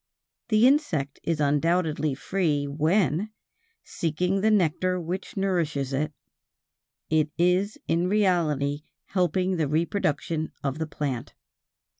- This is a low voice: No, medium, 165 Hz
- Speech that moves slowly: Yes, slow, 110 wpm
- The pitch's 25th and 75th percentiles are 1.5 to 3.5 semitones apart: No, average, 3.9 semitones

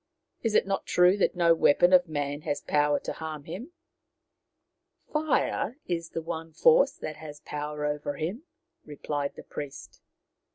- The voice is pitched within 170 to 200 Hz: No, medium, 160 Hz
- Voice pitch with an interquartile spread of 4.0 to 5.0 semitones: No, average, 3.5 semitones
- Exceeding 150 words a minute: Yes, average, 170 wpm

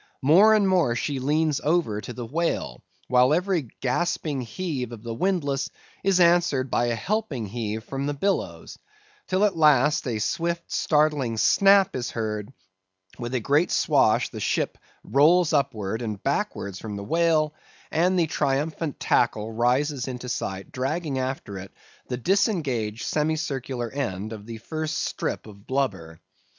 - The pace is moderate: Yes, average, 150 wpm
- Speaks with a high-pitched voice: No, low, 135 Hz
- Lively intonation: Yes, wide, 5.9 semitones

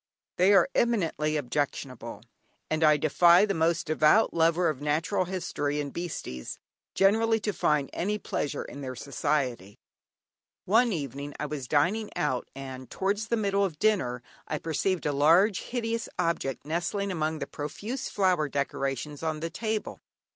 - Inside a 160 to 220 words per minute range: No, average, 150 wpm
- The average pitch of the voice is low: No, medium, 160 Hz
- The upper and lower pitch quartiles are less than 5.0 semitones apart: No, wide, 5.4 semitones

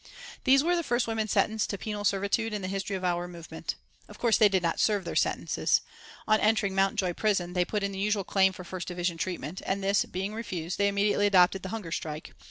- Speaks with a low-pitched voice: No, high, 195 Hz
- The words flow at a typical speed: No, fast, 225 wpm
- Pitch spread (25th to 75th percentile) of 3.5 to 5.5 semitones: No, average, 2.7 semitones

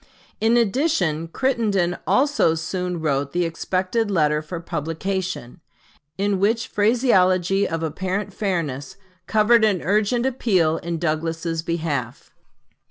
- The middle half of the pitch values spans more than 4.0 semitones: Yes, average, 4.5 semitones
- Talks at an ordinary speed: No, slow, 110 wpm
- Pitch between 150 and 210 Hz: Yes, medium, 185 Hz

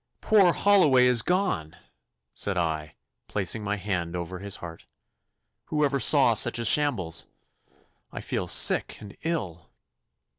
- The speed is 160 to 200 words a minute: No, slow, 135 wpm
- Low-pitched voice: Yes, low, 105 Hz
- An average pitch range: No, wide, 9.0 semitones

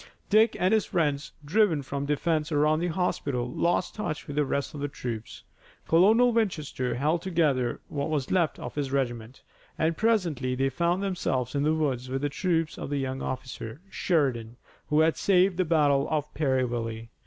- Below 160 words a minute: No, average, 180 wpm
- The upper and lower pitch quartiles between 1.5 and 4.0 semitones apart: No, average, 4.6 semitones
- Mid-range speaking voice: Yes, medium, 150 Hz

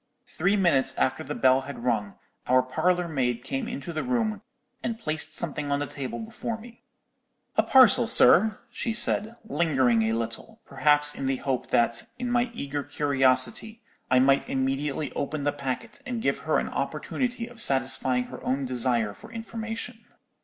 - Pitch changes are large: Yes, wide, 9.0 semitones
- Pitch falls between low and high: Yes, medium, 145 Hz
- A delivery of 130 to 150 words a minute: No, average, 165 wpm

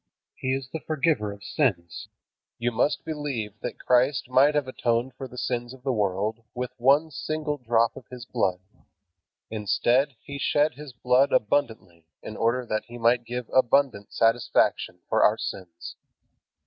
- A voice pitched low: Yes, low, 125 Hz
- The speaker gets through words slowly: No, average, 160 wpm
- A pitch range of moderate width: Yes, average, 3.5 semitones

